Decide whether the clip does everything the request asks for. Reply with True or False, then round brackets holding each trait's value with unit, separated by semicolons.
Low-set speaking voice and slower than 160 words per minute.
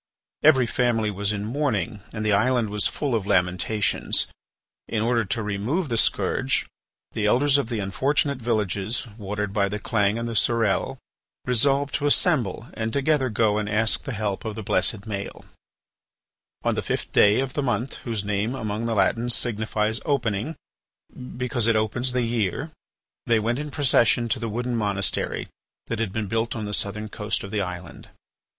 False (110 Hz; 175 wpm)